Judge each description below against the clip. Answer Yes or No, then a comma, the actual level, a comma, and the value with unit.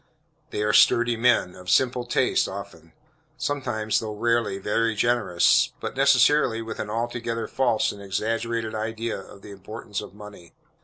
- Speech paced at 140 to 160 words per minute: Yes, average, 150 wpm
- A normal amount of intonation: No, narrow, 2.3 semitones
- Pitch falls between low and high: No, low, 115 Hz